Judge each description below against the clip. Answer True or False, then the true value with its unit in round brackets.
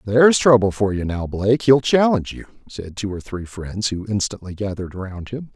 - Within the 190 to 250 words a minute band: True (205 wpm)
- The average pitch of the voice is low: True (105 Hz)